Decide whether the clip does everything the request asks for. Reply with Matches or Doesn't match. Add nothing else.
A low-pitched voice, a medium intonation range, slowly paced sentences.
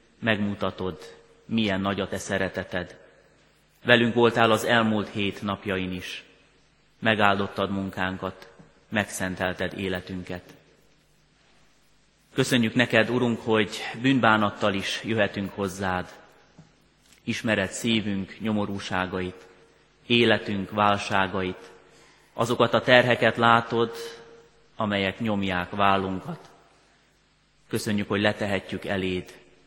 Matches